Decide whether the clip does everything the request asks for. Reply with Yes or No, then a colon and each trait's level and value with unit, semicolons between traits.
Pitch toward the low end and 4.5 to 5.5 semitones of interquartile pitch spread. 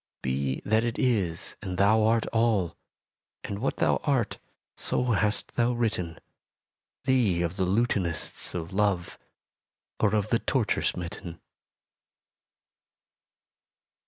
Yes: low, 100 Hz; average, 4.8 semitones